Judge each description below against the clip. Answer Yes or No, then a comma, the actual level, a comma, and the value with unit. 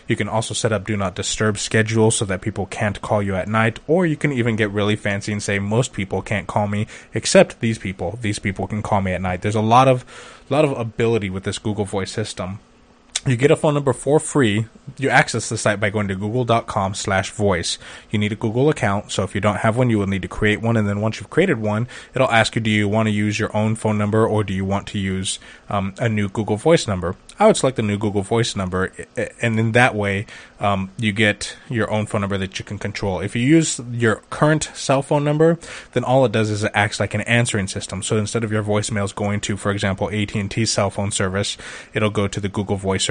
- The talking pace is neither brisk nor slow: No, fast, 245 wpm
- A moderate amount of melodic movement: No, narrow, 2.3 semitones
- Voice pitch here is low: Yes, low, 105 Hz